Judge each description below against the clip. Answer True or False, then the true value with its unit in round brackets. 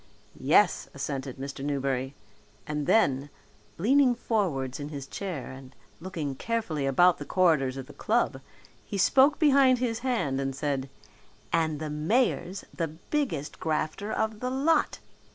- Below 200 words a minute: True (140 wpm)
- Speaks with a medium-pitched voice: True (160 Hz)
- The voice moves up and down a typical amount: False (8.5 semitones)